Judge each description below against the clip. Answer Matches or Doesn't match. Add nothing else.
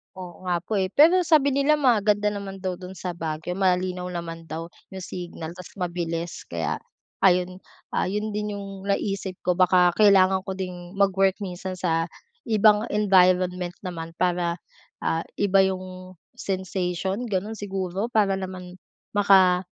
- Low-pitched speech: Doesn't match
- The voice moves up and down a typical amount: Doesn't match